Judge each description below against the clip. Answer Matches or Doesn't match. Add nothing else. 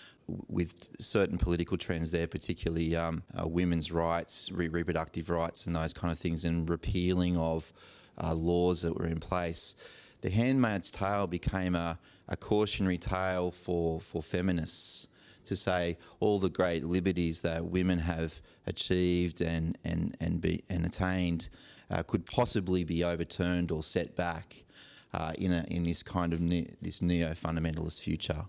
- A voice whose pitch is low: Matches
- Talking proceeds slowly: Doesn't match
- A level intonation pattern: Matches